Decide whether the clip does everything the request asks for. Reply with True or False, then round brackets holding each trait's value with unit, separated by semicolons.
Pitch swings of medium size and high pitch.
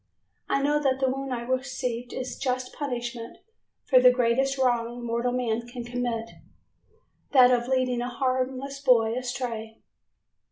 False (1.5 semitones; 250 Hz)